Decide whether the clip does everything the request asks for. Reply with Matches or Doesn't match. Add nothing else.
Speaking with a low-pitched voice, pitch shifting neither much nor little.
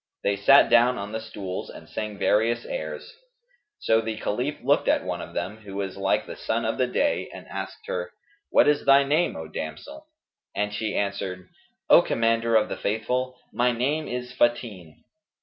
Matches